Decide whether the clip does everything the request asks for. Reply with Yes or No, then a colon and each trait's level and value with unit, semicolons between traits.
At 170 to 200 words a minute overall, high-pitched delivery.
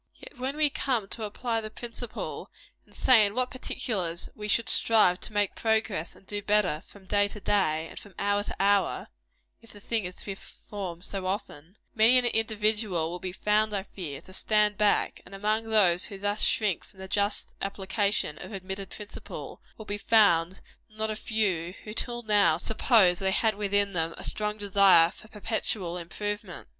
Yes: average, 190 wpm; high, 205 Hz